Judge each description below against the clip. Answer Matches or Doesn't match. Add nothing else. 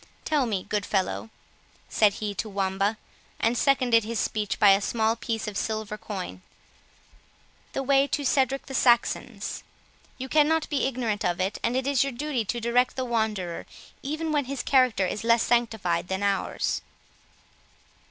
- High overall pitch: Matches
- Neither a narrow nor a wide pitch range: Matches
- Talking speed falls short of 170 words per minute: Matches